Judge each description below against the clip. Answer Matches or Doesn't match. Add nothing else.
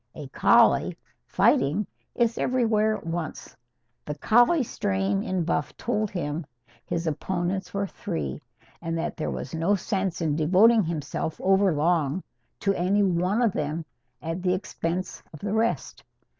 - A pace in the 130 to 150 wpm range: Matches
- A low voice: Doesn't match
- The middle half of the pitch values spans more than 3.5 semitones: Matches